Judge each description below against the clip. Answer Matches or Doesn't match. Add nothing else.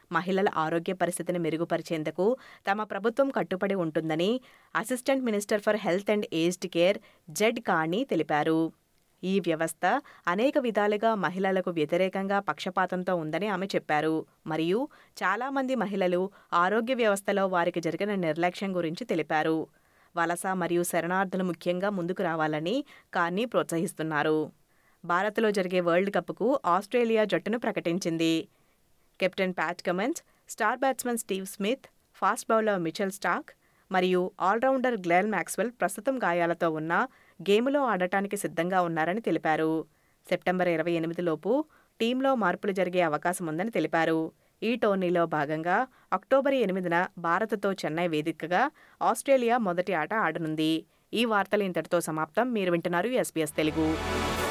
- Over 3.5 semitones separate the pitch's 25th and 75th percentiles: Matches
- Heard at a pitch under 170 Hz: Doesn't match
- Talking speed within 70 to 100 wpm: Doesn't match